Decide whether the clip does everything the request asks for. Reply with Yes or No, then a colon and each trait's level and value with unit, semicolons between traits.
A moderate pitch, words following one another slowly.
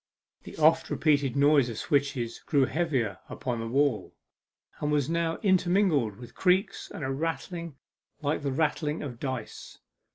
No: medium, 145 Hz; average, 150 wpm